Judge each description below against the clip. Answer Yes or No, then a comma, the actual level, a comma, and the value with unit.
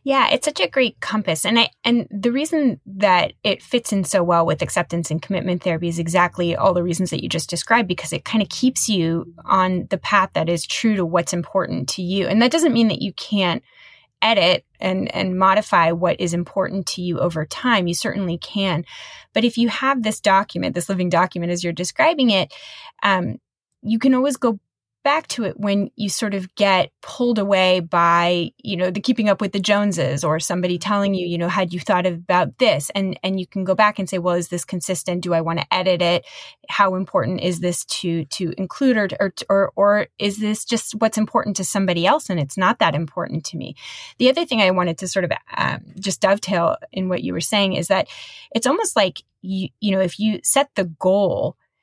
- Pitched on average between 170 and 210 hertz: Yes, high, 190 Hz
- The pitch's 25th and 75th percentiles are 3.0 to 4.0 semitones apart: Yes, average, 3.5 semitones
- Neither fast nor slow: No, fast, 220 wpm